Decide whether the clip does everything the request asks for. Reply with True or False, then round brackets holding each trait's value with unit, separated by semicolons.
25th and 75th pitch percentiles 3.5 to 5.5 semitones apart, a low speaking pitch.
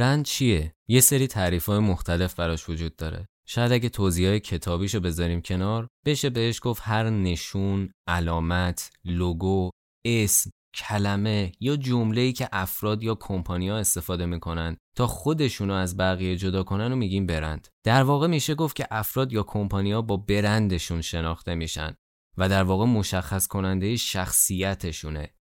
True (4.4 semitones; 95 Hz)